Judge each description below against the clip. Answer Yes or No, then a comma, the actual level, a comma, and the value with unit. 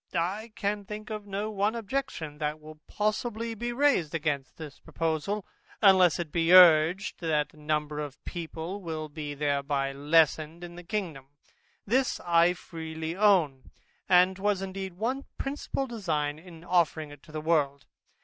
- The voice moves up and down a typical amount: Yes, average, 4.8 semitones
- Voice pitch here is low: No, medium, 170 Hz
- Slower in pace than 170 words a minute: Yes, average, 160 wpm